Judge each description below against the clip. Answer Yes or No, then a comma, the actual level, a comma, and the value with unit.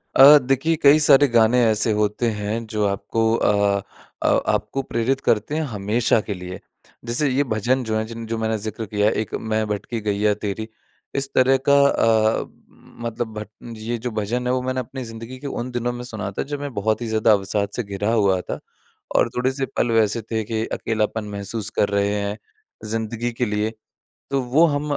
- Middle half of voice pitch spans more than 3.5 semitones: No, average, 2.9 semitones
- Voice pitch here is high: No, low, 115 Hz